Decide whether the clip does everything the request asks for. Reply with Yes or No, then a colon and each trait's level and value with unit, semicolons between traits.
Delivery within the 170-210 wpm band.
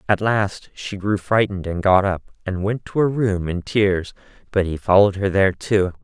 Yes: average, 200 wpm